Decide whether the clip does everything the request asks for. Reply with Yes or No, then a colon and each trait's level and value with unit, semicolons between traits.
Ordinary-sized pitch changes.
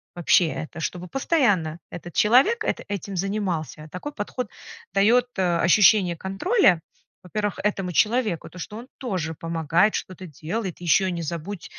Yes: average, 3.9 semitones